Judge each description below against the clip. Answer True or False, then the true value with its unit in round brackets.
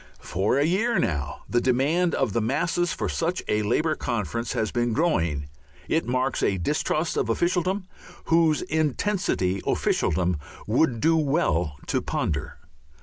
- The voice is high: False (130 Hz)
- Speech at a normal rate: True (145 wpm)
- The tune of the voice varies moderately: False (8.9 semitones)